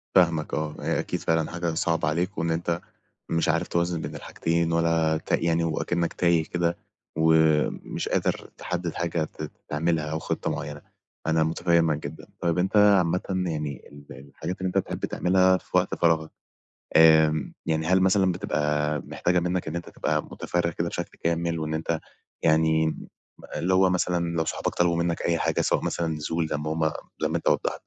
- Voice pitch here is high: No, very low, 85 Hz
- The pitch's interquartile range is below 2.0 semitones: Yes, narrow, 1.6 semitones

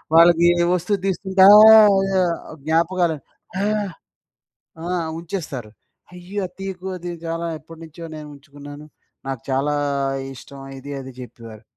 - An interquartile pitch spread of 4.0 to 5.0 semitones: Yes, average, 4.7 semitones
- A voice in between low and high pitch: Yes, medium, 170 Hz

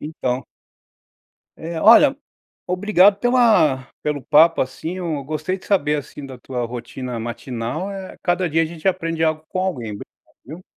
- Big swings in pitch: Yes, wide, 5.9 semitones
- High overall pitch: No, medium, 160 Hz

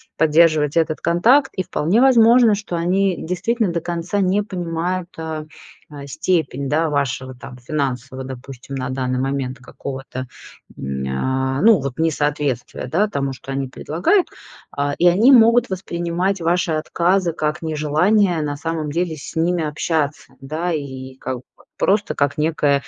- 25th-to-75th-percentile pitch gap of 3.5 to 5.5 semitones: Yes, average, 4.6 semitones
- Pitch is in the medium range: Yes, medium, 160 Hz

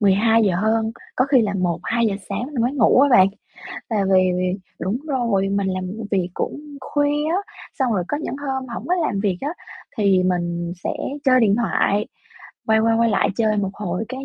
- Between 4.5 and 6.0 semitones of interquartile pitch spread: Yes, average, 4.9 semitones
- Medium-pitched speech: No, high, 220 Hz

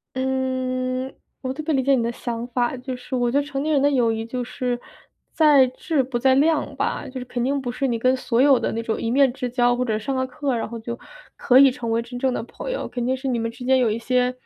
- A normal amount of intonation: No, narrow, 1.7 semitones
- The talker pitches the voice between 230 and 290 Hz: Yes, very high, 255 Hz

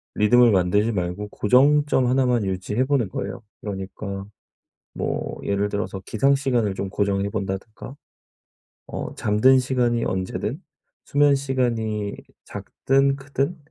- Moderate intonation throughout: Yes, average, 4.8 semitones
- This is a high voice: No, low, 110 Hz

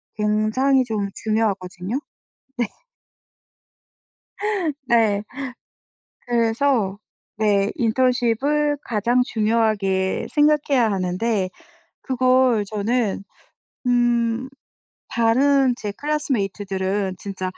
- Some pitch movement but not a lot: Yes, average, 3.9 semitones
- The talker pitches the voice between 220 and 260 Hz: Yes, high, 225 Hz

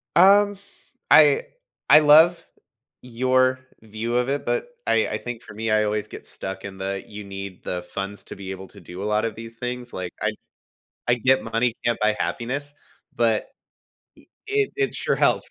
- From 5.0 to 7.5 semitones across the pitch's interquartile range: No, average, 4.5 semitones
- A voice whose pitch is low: Yes, low, 115 Hz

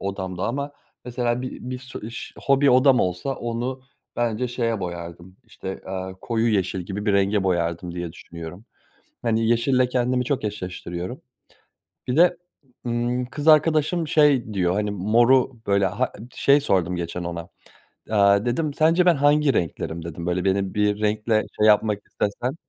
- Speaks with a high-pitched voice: No, low, 110 Hz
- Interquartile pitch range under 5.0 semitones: No, wide, 5.4 semitones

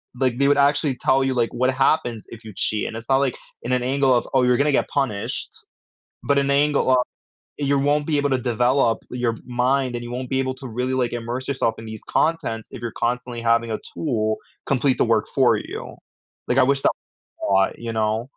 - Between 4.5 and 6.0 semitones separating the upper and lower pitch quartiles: No, average, 2.8 semitones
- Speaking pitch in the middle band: No, low, 125 Hz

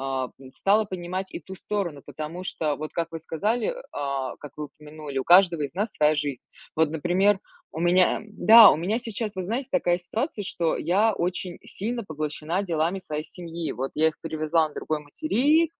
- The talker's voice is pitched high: No, medium, 170 Hz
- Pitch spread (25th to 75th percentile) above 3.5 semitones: Yes, average, 4.8 semitones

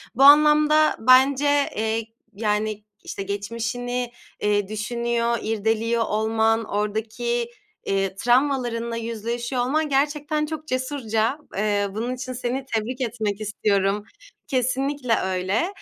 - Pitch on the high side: Yes, high, 235 Hz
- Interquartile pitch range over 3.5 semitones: No, average, 3.2 semitones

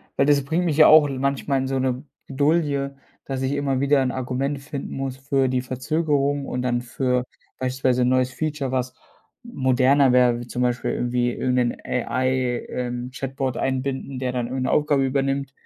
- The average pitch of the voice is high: No, low, 130 Hz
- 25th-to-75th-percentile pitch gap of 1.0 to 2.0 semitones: Yes, narrow, 1.7 semitones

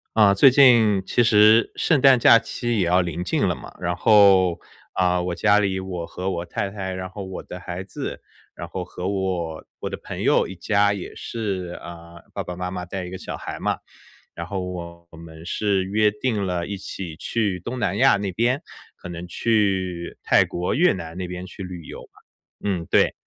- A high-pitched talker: No, very low, 95 Hz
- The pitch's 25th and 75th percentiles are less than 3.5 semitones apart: Yes, average, 2.8 semitones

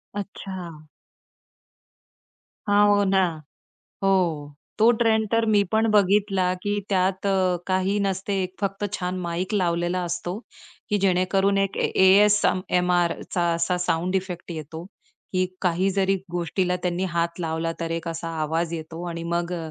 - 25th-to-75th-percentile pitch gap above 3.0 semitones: No, narrow, 2.4 semitones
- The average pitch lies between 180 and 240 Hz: Yes, medium, 185 Hz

